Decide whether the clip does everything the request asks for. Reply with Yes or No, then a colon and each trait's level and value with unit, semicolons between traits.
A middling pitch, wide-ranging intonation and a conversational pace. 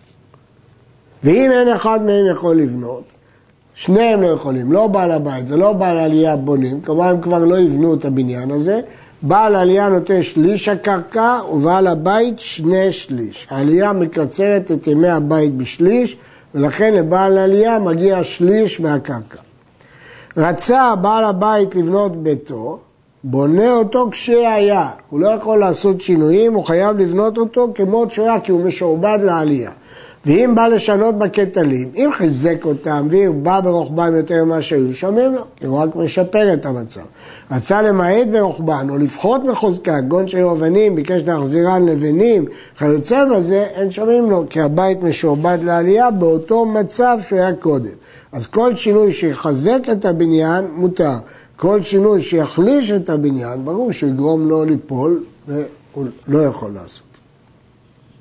Yes: medium, 175 Hz; wide, 5.7 semitones; average, 140 wpm